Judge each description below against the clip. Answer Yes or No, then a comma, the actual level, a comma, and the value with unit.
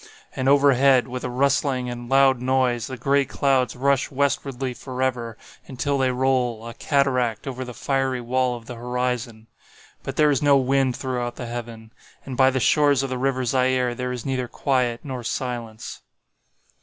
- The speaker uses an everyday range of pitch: No, narrow, 1.7 semitones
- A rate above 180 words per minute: No, average, 170 wpm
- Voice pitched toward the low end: Yes, low, 130 Hz